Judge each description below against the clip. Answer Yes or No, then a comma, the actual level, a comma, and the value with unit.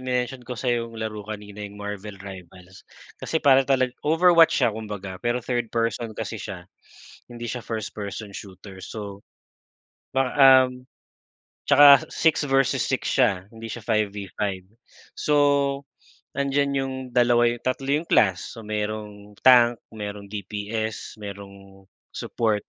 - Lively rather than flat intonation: No, average, 3.7 semitones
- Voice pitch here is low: Yes, low, 110 Hz